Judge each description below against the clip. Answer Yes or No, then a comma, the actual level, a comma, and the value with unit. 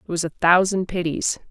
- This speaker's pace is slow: No, average, 200 wpm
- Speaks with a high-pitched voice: No, medium, 175 Hz